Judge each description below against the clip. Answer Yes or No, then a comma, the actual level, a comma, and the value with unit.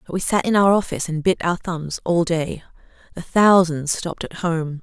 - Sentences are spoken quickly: Yes, fast, 210 wpm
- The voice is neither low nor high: Yes, medium, 170 Hz